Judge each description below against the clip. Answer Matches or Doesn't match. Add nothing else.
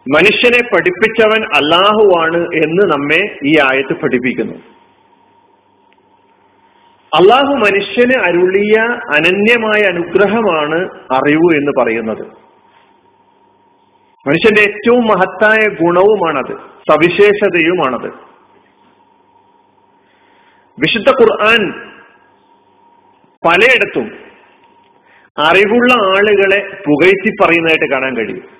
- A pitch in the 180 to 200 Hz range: Doesn't match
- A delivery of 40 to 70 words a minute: Matches